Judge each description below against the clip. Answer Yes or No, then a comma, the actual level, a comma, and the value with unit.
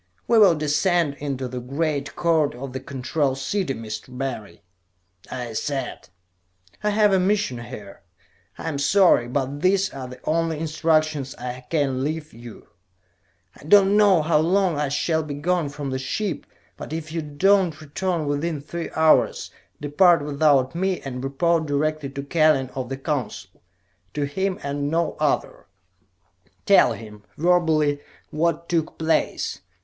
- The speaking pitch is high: No, medium, 150 Hz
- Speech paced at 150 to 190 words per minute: Yes, average, 155 wpm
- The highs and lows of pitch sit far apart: No, average, 3.8 semitones